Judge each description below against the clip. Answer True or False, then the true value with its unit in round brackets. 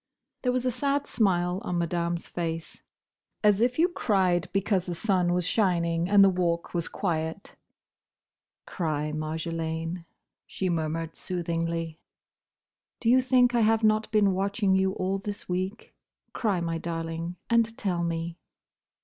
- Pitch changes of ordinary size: True (3.8 semitones)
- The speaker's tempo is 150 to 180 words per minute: False (140 wpm)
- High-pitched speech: False (180 Hz)